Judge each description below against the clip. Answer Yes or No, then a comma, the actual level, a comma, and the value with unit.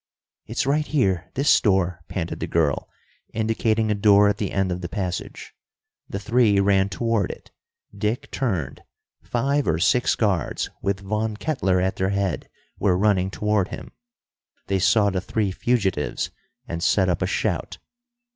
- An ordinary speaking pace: Yes, average, 155 wpm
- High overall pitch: No, low, 100 Hz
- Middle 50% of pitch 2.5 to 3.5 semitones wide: Yes, average, 2.9 semitones